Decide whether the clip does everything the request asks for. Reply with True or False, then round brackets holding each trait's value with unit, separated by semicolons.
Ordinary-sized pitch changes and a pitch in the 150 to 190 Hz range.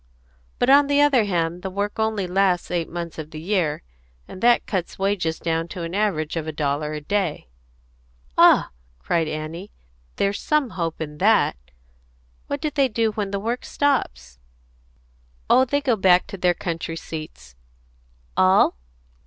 True (4.9 semitones; 185 Hz)